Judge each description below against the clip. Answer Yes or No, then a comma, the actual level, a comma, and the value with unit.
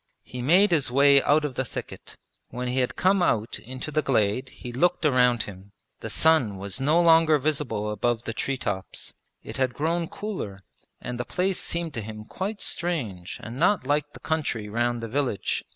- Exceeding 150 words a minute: Yes, average, 190 wpm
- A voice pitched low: Yes, low, 130 Hz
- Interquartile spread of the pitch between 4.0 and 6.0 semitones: Yes, wide, 5.6 semitones